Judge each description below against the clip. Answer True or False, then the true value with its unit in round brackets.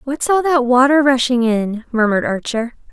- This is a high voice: True (255 Hz)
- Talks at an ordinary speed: True (165 wpm)